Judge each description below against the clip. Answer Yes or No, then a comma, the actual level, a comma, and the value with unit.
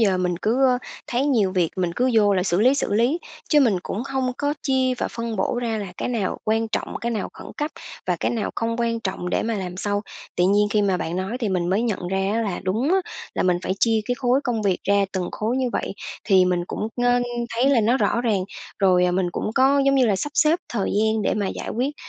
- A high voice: Yes, high, 220 Hz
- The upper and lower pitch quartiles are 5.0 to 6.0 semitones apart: No, average, 4.4 semitones